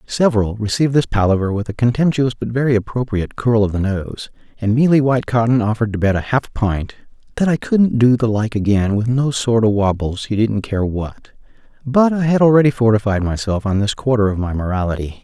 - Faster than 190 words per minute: Yes, average, 200 wpm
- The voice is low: Yes, low, 115 Hz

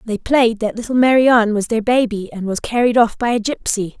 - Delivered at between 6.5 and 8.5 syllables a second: No, 5.4 syllables/s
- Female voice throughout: Yes, female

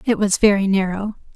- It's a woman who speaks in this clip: Yes, female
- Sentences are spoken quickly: No, average, 175 wpm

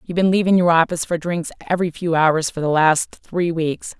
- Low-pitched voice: No, medium, 165 Hz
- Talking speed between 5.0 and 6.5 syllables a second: Yes, 5.4 syllables/s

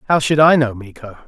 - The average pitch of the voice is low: Yes, low, 130 Hz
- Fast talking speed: Yes, fast, 235 wpm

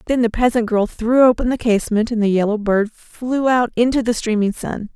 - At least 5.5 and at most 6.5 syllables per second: No, 5.3 syllables/s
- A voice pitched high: Yes, high, 230 Hz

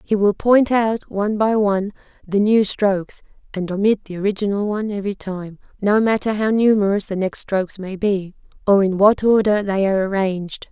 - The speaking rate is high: No, average, 185 wpm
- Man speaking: No, female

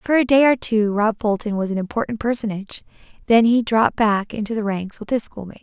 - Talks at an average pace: No, fast, 225 wpm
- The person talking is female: Yes, female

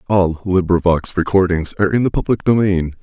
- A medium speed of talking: Yes, average, 160 wpm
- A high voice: No, very low, 90 Hz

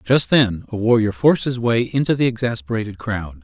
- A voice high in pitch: No, low, 115 Hz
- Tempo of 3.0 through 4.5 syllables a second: No, 5.5 syllables/s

